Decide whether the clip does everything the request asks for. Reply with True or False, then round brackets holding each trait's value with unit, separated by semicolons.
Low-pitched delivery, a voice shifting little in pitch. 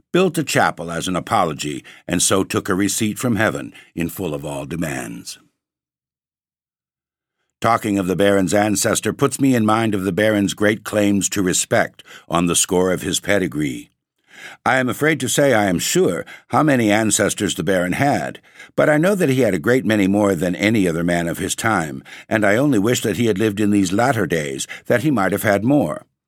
False (100 Hz; 3.6 semitones)